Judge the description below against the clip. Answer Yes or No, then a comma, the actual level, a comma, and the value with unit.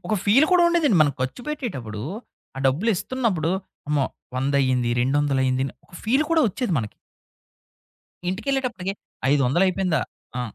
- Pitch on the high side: No, medium, 175 Hz